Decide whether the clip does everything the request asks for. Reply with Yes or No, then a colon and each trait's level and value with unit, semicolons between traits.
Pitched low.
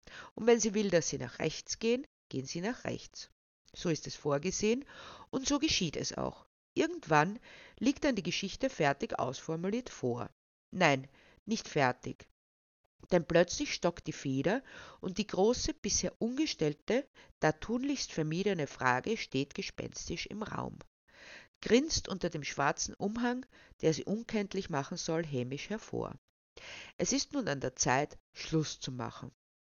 No: high, 190 Hz